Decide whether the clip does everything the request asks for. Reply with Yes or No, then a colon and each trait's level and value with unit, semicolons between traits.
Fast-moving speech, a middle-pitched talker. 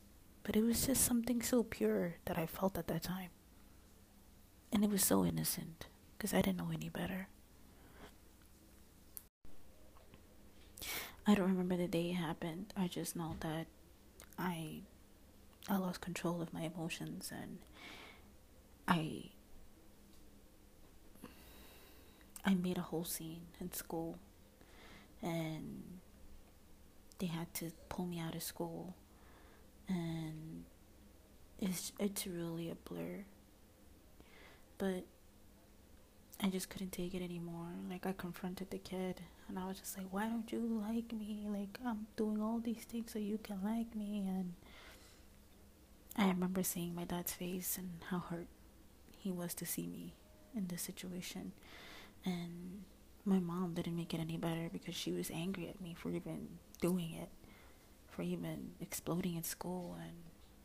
No: average, 140 wpm; medium, 175 Hz